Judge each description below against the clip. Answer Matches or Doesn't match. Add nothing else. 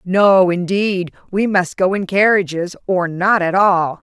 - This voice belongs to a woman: Matches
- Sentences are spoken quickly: Doesn't match